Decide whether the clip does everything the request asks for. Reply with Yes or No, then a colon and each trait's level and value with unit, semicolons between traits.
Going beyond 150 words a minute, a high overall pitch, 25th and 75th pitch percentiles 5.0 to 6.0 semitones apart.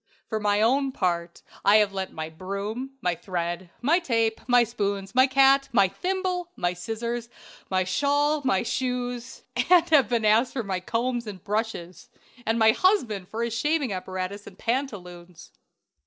Yes: average, 160 wpm; high, 225 Hz; wide, 5.4 semitones